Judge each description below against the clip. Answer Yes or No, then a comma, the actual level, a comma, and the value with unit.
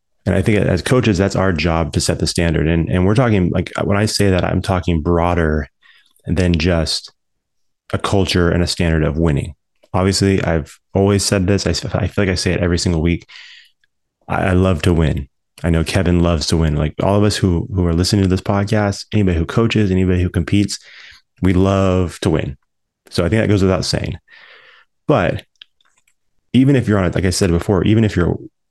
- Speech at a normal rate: No, fast, 210 wpm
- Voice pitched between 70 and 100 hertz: Yes, very low, 90 Hz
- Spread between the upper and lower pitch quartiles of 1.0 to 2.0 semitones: No, average, 2.9 semitones